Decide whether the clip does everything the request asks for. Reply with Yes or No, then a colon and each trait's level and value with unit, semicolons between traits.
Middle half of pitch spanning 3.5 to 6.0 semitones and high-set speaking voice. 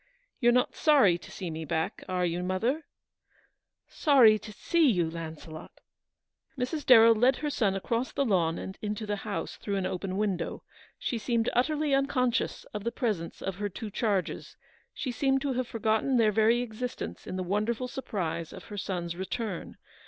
Yes: average, 5.1 semitones; high, 215 Hz